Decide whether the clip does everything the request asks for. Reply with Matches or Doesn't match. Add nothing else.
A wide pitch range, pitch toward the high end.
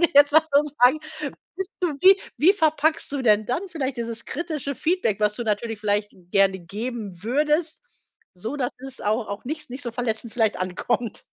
Matches